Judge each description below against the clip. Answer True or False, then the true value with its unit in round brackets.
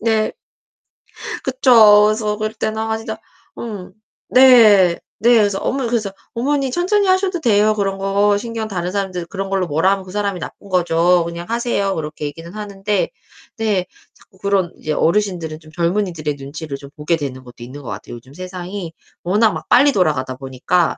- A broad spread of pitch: False (4.5 semitones)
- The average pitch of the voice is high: True (195 Hz)